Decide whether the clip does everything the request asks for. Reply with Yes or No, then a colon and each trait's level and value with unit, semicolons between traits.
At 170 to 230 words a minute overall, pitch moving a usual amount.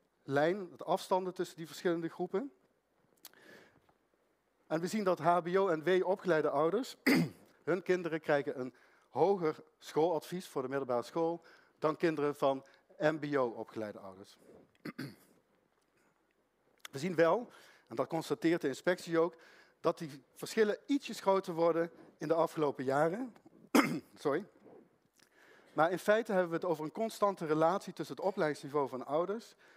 No: slow, 135 wpm; average, 3.8 semitones